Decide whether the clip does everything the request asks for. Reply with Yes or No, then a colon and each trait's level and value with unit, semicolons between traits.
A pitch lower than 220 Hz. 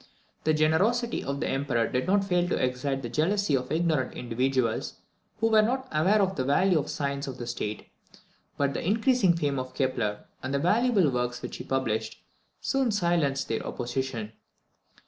Yes: medium, 140 Hz